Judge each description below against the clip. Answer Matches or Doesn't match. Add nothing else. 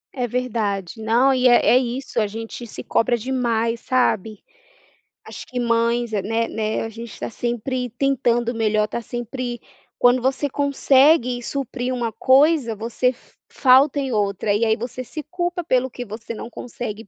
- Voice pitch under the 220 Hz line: Doesn't match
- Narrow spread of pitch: Matches